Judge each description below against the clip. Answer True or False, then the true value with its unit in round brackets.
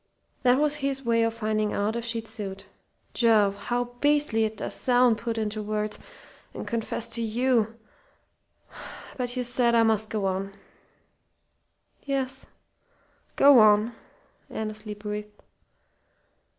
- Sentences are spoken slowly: True (125 wpm)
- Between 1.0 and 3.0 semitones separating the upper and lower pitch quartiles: True (2.4 semitones)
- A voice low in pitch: False (225 Hz)